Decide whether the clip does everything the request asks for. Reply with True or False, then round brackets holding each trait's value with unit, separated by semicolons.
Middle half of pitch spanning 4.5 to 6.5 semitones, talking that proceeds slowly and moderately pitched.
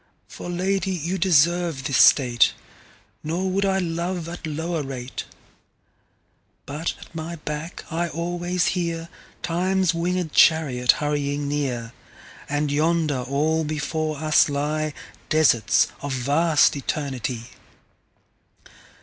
False (3.2 semitones; 95 wpm; 155 Hz)